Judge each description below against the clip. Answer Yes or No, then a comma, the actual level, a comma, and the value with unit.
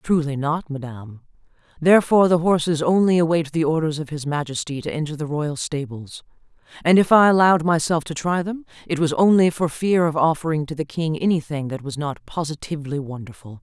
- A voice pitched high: No, medium, 155 Hz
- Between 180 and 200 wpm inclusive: Yes, average, 185 wpm